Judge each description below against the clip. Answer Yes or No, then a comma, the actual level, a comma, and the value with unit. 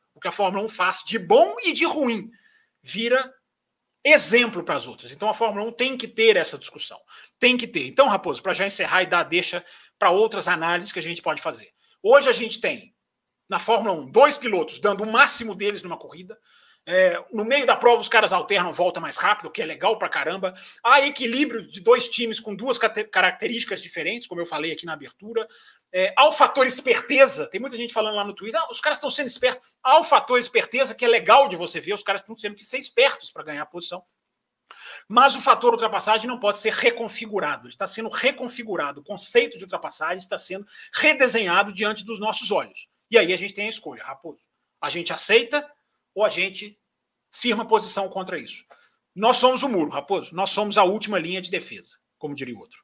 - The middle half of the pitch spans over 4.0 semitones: Yes, average, 5.2 semitones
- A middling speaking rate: No, fast, 210 wpm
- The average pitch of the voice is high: Yes, high, 220 Hz